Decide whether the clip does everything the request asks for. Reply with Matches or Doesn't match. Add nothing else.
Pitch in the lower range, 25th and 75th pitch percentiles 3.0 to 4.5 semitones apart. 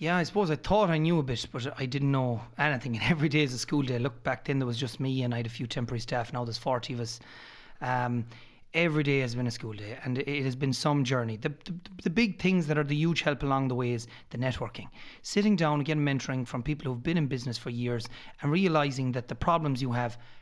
Matches